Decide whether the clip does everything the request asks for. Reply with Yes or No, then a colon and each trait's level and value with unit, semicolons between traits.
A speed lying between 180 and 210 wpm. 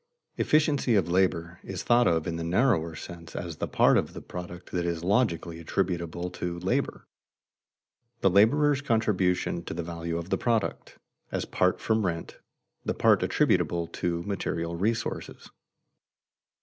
No: average, 150 wpm